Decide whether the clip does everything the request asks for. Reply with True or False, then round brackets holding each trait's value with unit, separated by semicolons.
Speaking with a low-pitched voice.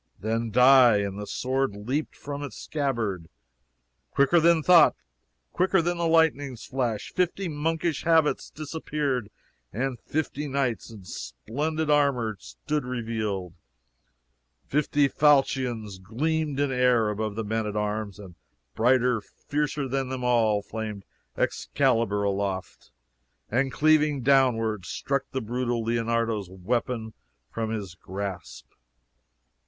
True (125 Hz)